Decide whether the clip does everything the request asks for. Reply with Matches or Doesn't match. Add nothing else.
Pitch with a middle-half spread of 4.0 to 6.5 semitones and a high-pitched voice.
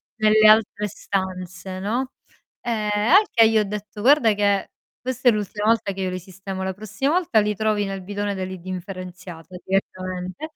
Doesn't match